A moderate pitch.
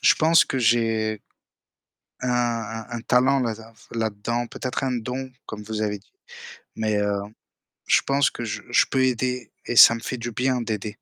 No: low, 115 Hz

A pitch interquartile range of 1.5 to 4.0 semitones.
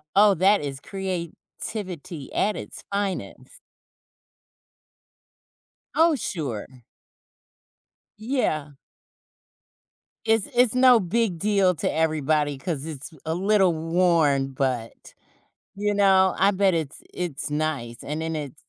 No: average, 5.2 semitones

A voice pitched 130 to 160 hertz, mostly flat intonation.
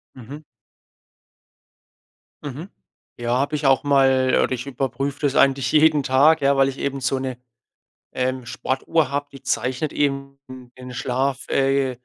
Yes: low, 135 Hz; narrow, 1.4 semitones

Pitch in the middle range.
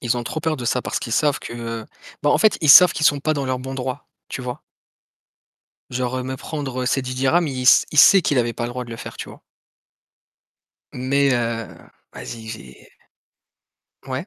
No: low, 130 Hz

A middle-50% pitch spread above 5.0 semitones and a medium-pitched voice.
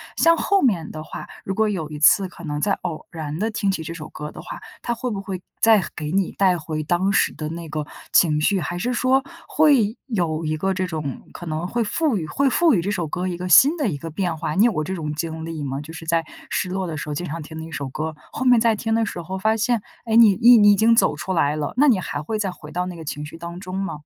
Yes: wide, 5.4 semitones; medium, 180 Hz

